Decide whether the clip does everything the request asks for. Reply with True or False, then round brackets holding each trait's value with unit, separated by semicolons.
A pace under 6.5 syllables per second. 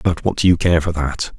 True (5.5 syllables/s)